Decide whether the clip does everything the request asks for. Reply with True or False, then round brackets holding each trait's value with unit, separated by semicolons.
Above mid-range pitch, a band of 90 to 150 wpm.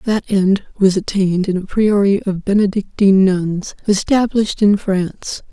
True (195 Hz; 140 wpm)